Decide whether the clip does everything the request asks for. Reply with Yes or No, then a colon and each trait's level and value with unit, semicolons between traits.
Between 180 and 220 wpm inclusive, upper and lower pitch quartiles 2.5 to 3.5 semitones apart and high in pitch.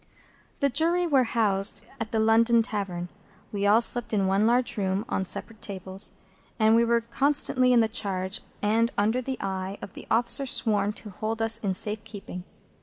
Yes: average, 185 wpm; average, 2.9 semitones; high, 220 Hz